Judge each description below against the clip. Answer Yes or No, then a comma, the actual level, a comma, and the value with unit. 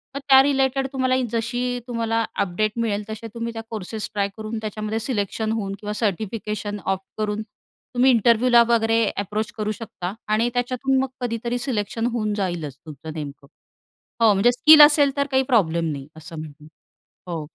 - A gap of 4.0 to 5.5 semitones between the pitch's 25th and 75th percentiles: No, average, 3.2 semitones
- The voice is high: Yes, high, 220 Hz